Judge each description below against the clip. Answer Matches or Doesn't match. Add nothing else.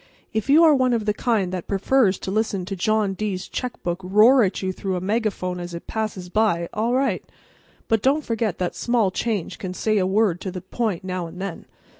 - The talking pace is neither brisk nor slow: Doesn't match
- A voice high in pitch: Matches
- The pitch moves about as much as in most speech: Matches